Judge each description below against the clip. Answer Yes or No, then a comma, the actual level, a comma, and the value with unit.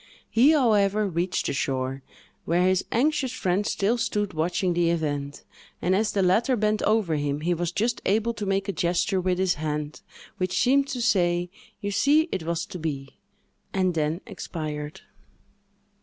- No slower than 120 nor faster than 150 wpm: No, average, 170 wpm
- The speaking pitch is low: No, medium, 185 Hz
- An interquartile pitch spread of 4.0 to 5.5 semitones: Yes, average, 4.6 semitones